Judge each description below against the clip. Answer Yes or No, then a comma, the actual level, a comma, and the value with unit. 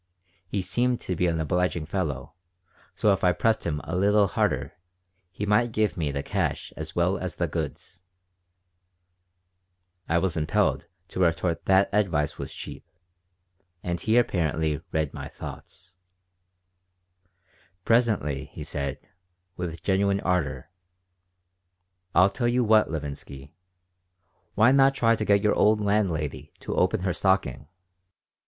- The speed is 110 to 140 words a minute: Yes, slow, 135 wpm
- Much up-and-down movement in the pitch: No, average, 4.9 semitones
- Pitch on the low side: Yes, very low, 90 Hz